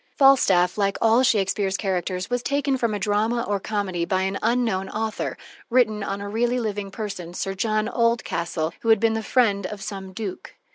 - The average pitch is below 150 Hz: No, high, 210 Hz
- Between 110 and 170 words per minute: No, average, 185 wpm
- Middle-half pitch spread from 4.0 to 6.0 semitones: No, average, 3.1 semitones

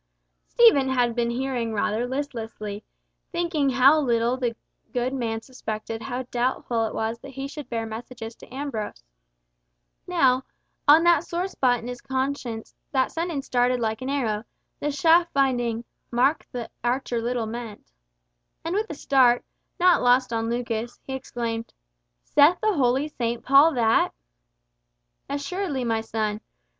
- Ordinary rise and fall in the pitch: Yes, average, 3.4 semitones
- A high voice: Yes, very high, 250 Hz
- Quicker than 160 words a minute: No, average, 145 wpm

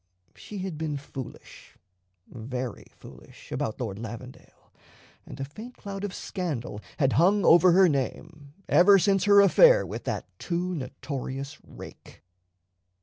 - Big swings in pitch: Yes, wide, 6.5 semitones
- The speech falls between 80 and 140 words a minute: Yes, slow, 135 wpm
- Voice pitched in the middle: Yes, medium, 160 Hz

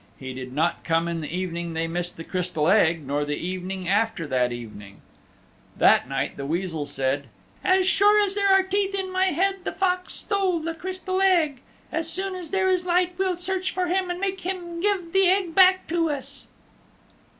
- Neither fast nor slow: Yes, average, 195 wpm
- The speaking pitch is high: Yes, very high, 335 Hz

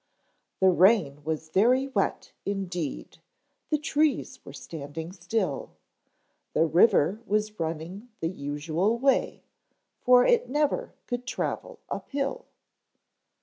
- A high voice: Yes, high, 195 Hz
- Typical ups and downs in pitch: No, wide, 7.6 semitones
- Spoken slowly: Yes, slow, 110 wpm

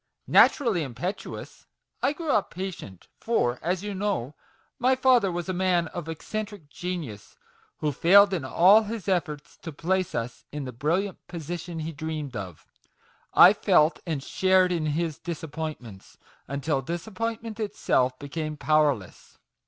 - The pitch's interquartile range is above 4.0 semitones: Yes, average, 4.7 semitones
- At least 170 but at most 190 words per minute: No, average, 145 wpm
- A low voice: No, medium, 170 Hz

